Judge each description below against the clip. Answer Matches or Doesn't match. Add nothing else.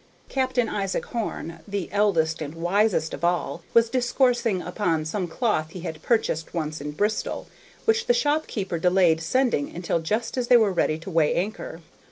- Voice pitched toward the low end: Doesn't match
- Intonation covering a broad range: Matches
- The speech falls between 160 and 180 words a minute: Matches